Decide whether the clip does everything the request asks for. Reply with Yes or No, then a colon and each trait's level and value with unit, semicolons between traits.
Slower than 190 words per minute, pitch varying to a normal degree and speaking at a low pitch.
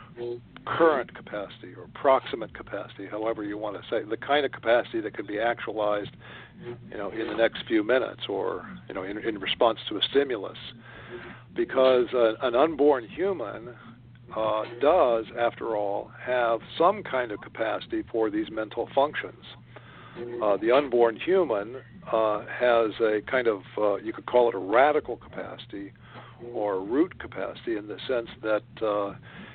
Yes: average, 155 wpm; average, 3.2 semitones; low, 120 Hz